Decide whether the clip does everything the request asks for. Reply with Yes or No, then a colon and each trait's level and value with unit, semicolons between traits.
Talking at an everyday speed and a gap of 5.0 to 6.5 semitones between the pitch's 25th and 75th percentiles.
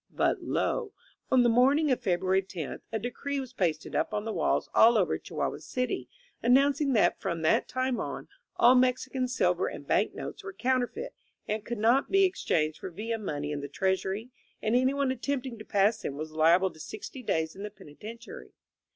Yes: average, 195 wpm; wide, 5.4 semitones